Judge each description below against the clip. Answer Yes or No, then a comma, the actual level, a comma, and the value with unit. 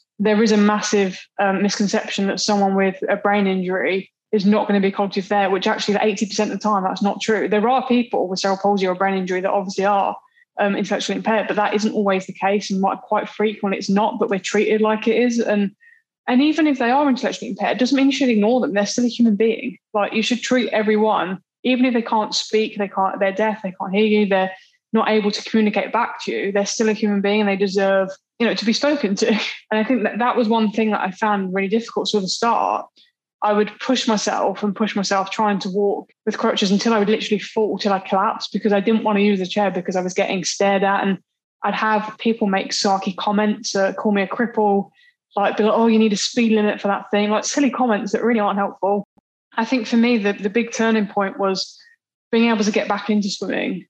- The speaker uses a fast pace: Yes, fast, 245 wpm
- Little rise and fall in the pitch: Yes, narrow, 2.0 semitones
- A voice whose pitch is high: Yes, high, 210 Hz